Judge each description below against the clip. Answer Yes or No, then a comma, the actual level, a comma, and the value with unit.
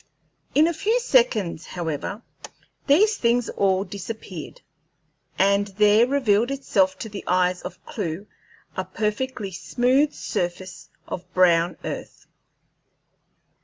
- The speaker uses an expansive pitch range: Yes, wide, 5.7 semitones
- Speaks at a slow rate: Yes, slow, 110 wpm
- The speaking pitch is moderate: No, high, 205 Hz